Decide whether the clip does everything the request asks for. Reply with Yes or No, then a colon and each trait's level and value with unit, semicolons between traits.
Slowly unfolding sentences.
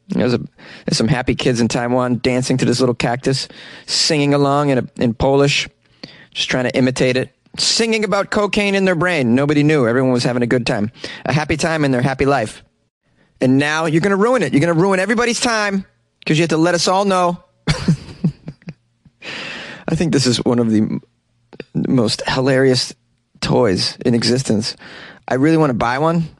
No: average, 190 wpm